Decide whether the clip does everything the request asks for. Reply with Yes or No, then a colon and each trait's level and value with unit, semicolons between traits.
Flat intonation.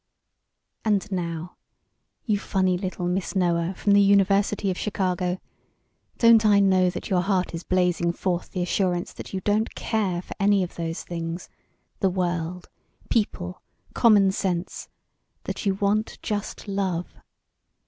Yes: narrow, 2.1 semitones